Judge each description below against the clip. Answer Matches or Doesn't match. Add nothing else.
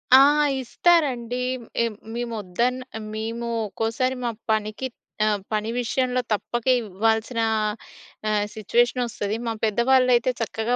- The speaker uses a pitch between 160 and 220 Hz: Doesn't match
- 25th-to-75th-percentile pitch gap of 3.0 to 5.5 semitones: Doesn't match